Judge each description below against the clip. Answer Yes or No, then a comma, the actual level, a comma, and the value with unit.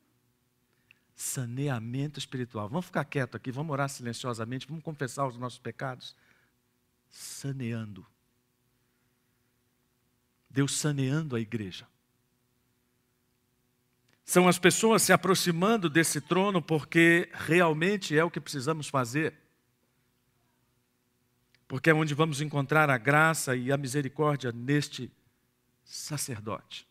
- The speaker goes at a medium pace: No, slow, 100 wpm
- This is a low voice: Yes, low, 130 Hz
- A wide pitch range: No, average, 4.1 semitones